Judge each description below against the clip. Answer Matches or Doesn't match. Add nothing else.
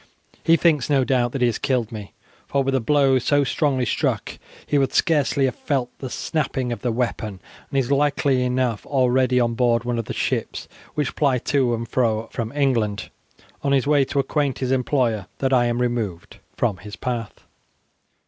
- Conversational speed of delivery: Matches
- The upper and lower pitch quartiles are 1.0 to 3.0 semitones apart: Matches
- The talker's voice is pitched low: Matches